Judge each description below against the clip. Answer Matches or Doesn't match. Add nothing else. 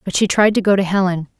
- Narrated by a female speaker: Matches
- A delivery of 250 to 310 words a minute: Matches